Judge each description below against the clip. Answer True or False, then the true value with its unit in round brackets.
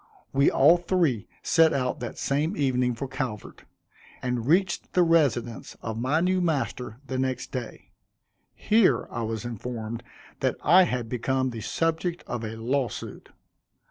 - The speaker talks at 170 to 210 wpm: False (150 wpm)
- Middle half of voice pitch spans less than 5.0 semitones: False (5.5 semitones)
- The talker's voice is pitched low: True (130 Hz)